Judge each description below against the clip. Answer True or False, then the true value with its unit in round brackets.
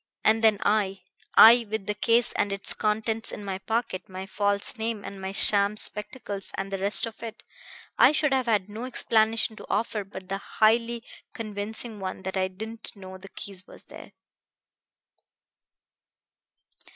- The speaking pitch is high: True (210 Hz)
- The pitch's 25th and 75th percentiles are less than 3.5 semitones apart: True (2.4 semitones)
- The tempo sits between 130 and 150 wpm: False (165 wpm)